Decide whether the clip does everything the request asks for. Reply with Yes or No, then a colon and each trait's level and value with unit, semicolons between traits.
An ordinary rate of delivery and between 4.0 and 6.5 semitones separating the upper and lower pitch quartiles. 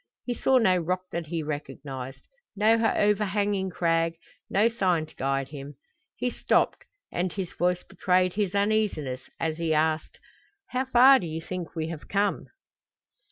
Yes: average, 155 wpm; average, 4.5 semitones